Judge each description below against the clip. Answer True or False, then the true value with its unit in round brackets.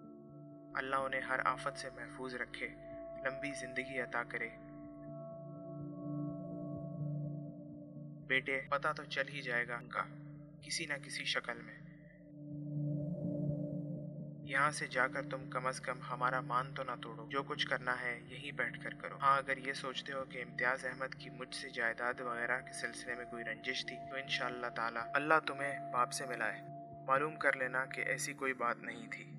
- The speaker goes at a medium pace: True (165 wpm)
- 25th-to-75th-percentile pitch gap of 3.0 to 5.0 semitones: False (2.6 semitones)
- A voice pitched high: False (140 Hz)